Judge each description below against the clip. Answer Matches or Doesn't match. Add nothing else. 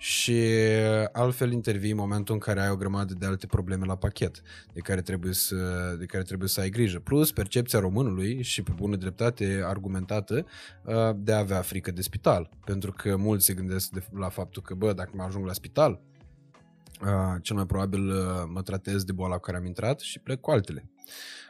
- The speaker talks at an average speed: Doesn't match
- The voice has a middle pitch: Doesn't match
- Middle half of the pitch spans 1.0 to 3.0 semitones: Matches